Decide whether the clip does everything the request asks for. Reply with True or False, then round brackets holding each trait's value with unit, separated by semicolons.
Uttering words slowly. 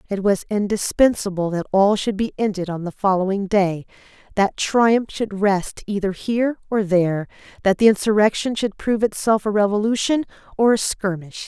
False (160 wpm)